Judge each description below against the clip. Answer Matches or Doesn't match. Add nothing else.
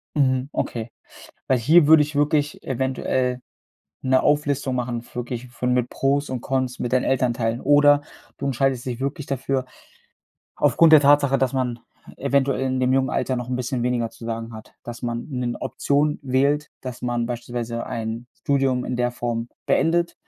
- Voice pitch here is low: Matches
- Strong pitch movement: Doesn't match